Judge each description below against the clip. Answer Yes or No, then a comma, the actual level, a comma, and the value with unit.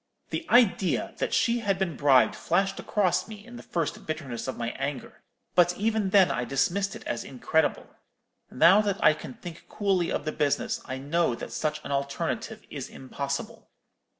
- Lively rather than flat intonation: Yes, wide, 6.0 semitones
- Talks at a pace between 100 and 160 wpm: No, average, 175 wpm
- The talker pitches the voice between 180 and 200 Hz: No, medium, 165 Hz